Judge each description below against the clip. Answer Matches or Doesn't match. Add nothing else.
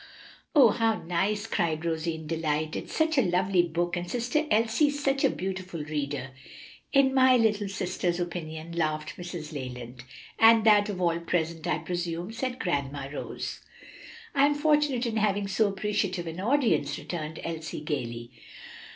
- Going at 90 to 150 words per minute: Doesn't match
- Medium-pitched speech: Matches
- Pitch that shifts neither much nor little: Doesn't match